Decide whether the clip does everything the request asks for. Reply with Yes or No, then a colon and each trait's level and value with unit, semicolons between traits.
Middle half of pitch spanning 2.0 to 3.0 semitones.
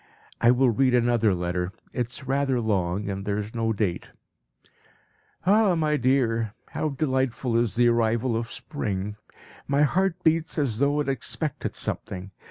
No: average, 4.7 semitones